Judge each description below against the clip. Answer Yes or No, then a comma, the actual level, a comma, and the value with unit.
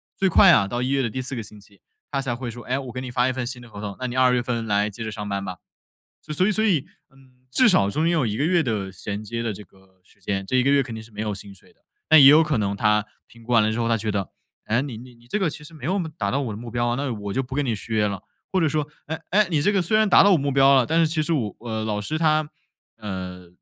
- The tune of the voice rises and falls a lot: Yes, wide, 5.7 semitones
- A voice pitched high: No, low, 125 Hz